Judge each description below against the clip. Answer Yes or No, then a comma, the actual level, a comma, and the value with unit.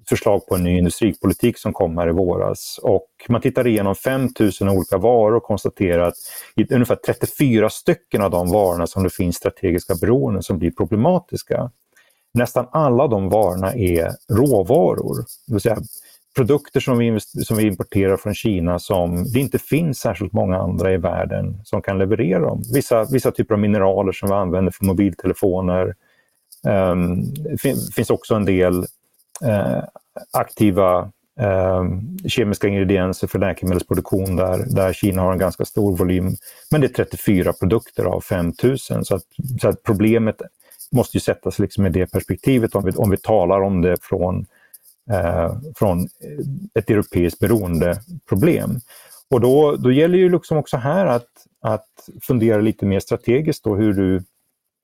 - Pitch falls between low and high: No, low, 100 Hz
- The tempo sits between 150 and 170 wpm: Yes, average, 160 wpm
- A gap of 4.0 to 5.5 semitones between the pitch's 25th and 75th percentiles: Yes, average, 4.3 semitones